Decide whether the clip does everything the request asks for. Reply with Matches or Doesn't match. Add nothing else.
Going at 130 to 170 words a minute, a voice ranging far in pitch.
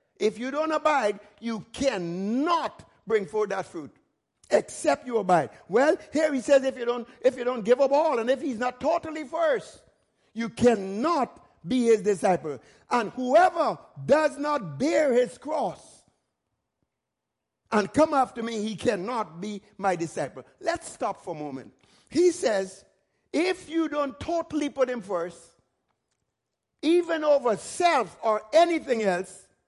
Matches